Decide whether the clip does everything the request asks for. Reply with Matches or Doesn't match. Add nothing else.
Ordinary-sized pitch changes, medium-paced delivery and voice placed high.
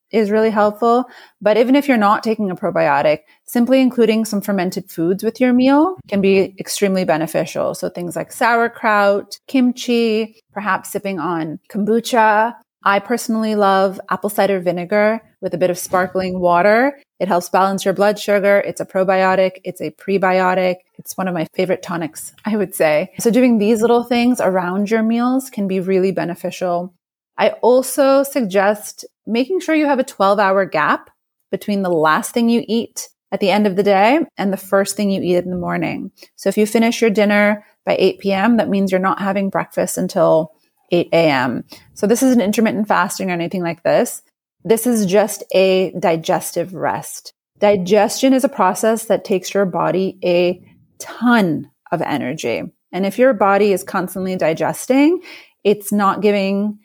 Matches